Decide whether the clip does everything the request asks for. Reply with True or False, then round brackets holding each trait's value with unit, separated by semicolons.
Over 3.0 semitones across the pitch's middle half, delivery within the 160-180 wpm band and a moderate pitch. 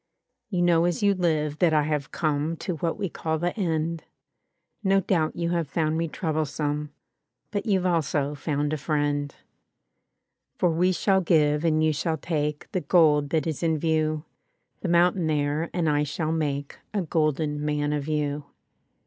False (2.4 semitones; 170 wpm; 155 Hz)